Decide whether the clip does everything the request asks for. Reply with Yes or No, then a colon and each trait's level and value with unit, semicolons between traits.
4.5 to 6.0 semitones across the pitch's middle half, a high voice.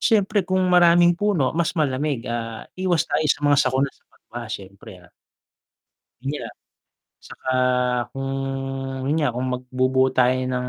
No: average, 5.1 semitones; low, 135 Hz